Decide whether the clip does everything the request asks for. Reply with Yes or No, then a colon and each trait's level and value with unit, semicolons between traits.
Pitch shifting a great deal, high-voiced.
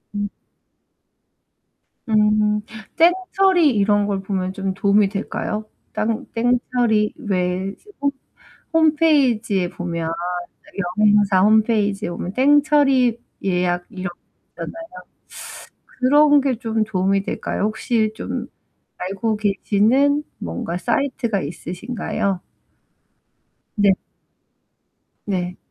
No: average, 4.5 semitones; high, 210 Hz